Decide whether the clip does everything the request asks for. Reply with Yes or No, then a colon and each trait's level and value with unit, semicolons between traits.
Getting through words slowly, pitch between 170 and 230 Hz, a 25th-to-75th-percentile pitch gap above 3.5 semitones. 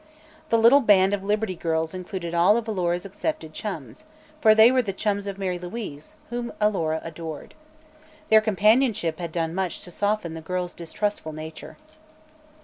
No: average, 160 wpm; high, 190 Hz; average, 4.2 semitones